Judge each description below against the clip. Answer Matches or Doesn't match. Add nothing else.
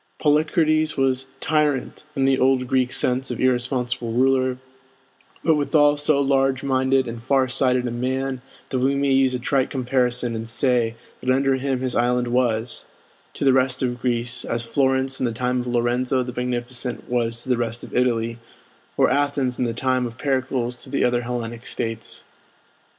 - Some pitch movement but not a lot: Doesn't match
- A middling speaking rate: Matches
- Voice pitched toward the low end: Matches